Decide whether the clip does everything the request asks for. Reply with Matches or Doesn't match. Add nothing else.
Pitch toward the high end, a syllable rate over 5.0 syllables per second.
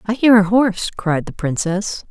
Doesn't match